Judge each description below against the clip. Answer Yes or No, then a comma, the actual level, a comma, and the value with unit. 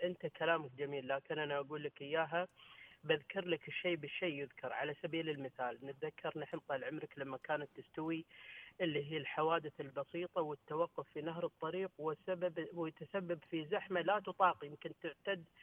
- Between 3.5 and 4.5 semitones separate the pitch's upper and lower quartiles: No, average, 3.1 semitones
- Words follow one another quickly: Yes, fast, 150 wpm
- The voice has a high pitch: No, medium, 160 Hz